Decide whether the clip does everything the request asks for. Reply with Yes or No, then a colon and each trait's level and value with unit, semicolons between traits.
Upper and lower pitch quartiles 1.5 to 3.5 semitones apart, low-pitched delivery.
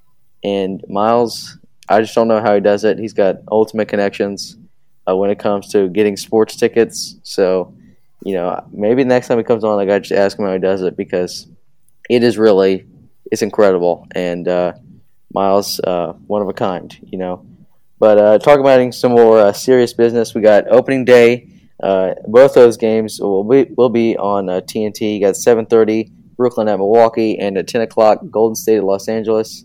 Yes: average, 2.9 semitones; low, 110 Hz